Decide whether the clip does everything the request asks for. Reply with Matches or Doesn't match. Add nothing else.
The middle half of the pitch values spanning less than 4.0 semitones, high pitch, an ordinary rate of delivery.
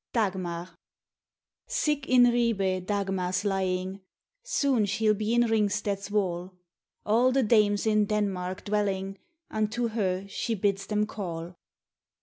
Doesn't match